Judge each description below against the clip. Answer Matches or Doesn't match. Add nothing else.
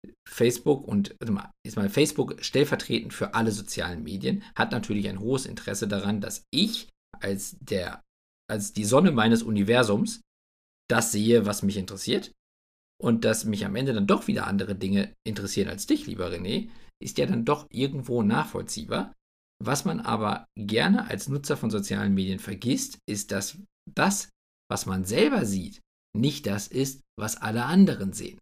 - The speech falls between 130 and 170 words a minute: Matches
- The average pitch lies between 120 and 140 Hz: Doesn't match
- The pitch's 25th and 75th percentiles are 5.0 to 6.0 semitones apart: Matches